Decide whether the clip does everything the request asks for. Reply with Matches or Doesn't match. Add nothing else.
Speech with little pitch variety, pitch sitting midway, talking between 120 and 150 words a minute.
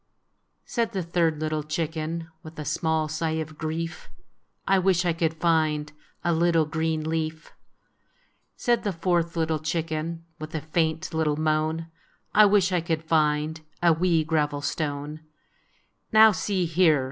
Doesn't match